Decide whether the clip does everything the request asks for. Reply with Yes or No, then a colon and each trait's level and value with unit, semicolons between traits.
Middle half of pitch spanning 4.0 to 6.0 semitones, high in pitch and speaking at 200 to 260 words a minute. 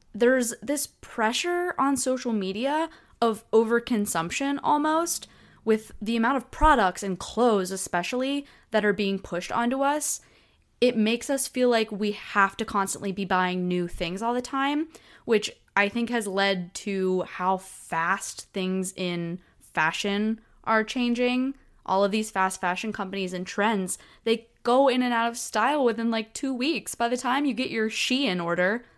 No: average, 4.6 semitones; high, 225 Hz; average, 165 wpm